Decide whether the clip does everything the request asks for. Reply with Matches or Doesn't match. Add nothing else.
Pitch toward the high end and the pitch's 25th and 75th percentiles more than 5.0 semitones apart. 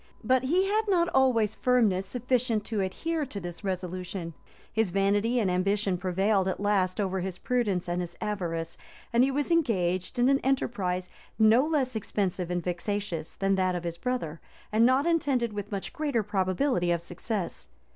Matches